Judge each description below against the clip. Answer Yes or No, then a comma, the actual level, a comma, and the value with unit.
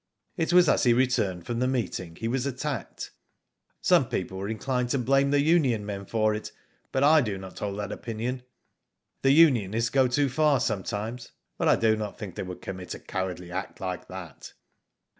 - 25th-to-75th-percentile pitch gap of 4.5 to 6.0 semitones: Yes, average, 5.3 semitones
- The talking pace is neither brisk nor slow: Yes, average, 190 wpm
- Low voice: Yes, low, 115 Hz